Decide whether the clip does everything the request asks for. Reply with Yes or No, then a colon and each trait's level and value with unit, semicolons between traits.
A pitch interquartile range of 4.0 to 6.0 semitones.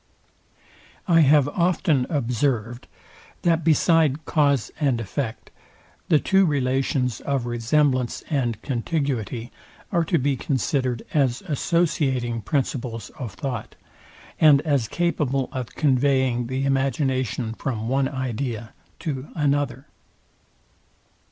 No: average, 3.3 semitones